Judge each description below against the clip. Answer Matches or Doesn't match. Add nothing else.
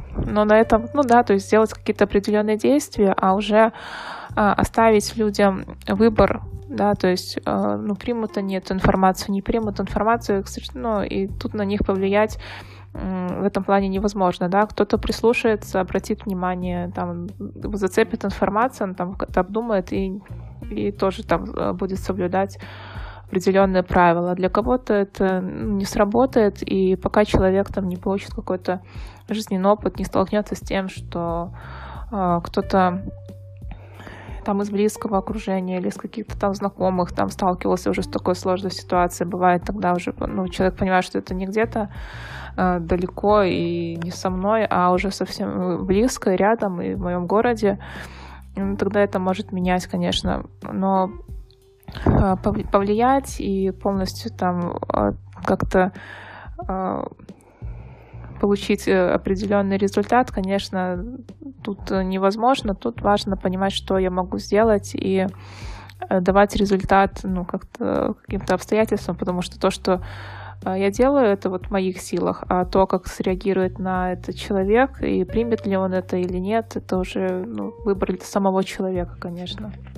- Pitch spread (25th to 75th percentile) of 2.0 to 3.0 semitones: Matches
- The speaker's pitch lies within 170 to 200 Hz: Matches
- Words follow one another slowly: Doesn't match